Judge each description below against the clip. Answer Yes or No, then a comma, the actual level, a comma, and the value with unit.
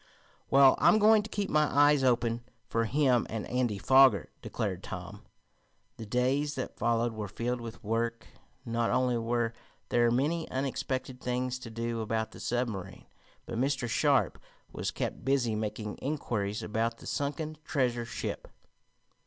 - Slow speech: No, average, 150 wpm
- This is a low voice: Yes, low, 120 Hz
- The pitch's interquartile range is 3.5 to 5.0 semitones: No, average, 2.9 semitones